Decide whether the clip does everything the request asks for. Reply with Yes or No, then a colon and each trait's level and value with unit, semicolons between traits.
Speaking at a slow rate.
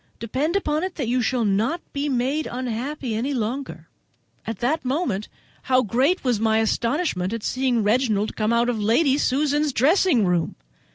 No: average, 165 wpm